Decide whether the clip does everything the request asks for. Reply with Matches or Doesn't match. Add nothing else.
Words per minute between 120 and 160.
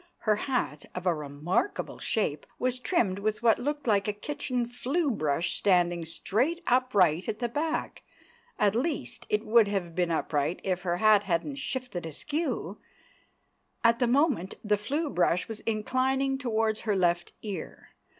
Matches